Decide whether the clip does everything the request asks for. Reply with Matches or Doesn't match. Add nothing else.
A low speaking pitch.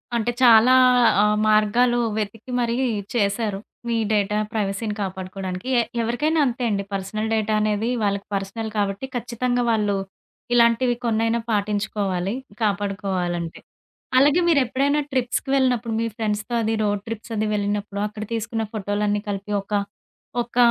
Doesn't match